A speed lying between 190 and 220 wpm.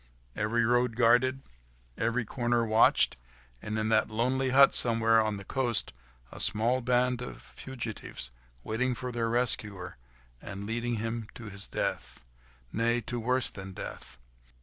No: average, 140 wpm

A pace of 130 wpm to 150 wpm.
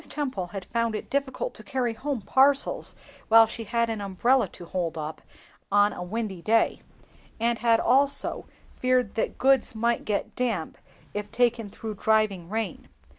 No: average, 160 wpm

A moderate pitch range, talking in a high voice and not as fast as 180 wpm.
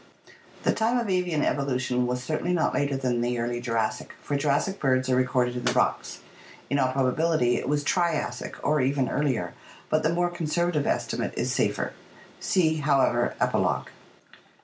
No: average, 4.2 semitones; medium, 140 Hz; average, 170 wpm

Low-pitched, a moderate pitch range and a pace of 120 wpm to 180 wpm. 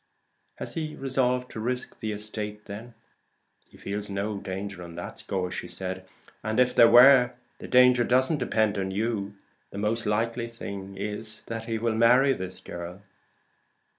Yes: low, 110 Hz; average, 3.5 semitones; average, 160 wpm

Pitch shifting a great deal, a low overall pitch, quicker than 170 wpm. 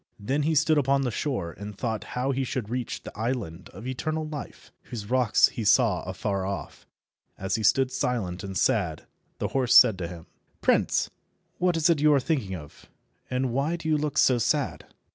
Yes: wide, 5.7 semitones; low, 125 Hz; average, 195 wpm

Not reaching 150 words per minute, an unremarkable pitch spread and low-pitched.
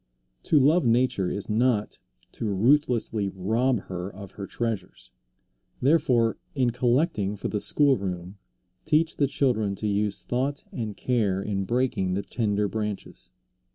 Yes: average, 140 wpm; average, 4.4 semitones; low, 110 Hz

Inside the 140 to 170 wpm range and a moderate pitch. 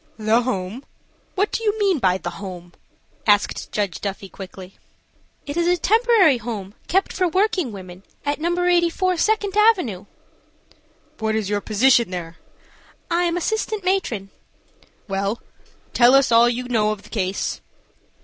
No: average, 150 wpm; high, 240 Hz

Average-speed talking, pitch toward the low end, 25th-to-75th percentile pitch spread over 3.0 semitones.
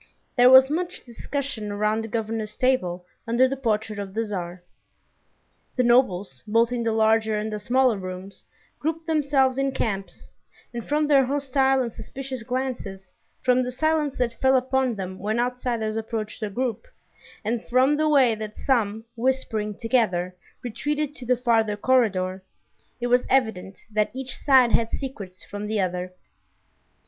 No: average, 155 wpm; high, 235 Hz; average, 3.7 semitones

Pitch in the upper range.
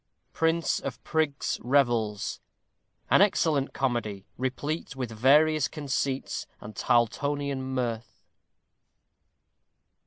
No: low, 135 Hz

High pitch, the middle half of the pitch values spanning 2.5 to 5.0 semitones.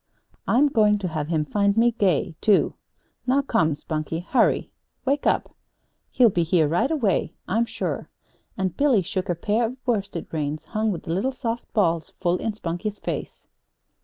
No: high, 200 Hz; wide, 5.5 semitones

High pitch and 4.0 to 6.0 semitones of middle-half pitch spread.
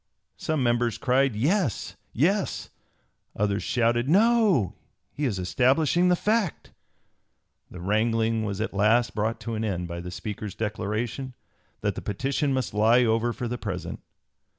No: low, 115 Hz; average, 4.5 semitones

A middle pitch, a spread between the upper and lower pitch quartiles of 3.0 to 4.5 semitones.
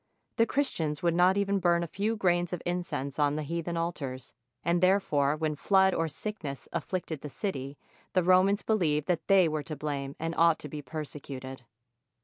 Yes: medium, 165 Hz; average, 3.8 semitones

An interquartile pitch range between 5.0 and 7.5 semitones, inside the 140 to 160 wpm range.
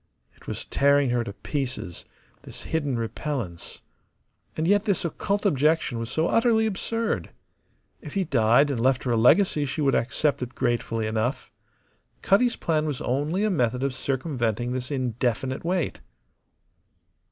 Yes: average, 5.3 semitones; average, 150 wpm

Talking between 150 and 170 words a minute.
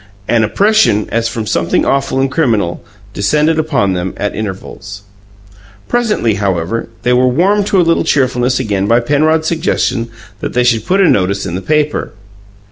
Yes: average, 165 wpm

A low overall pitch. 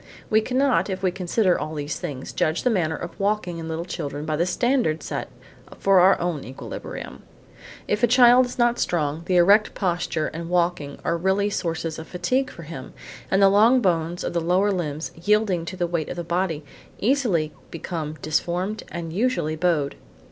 No: medium, 175 Hz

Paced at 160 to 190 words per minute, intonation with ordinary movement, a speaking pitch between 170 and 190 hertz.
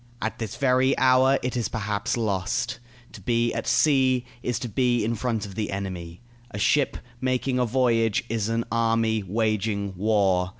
No: average, 170 wpm; average, 3.4 semitones; low, 115 Hz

